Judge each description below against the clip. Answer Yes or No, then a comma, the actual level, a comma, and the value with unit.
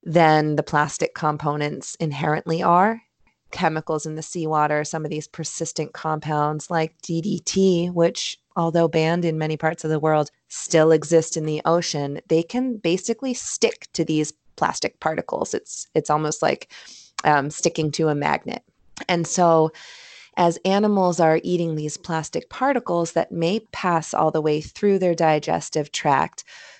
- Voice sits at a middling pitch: Yes, medium, 160 Hz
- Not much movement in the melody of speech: Yes, narrow, 2.1 semitones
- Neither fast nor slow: Yes, average, 150 wpm